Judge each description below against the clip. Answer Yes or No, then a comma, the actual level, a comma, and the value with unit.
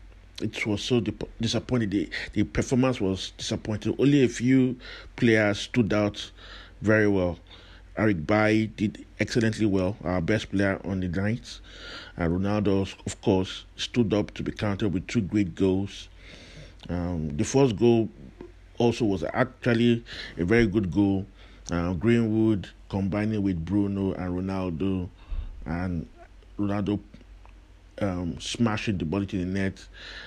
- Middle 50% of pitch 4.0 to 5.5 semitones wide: No, average, 3.2 semitones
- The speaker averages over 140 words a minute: No, slow, 135 wpm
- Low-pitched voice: Yes, low, 100 Hz